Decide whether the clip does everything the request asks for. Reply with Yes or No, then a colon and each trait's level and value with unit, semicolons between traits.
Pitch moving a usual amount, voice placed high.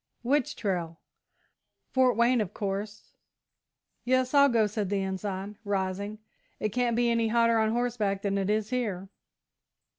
Yes: average, 3.3 semitones; high, 215 Hz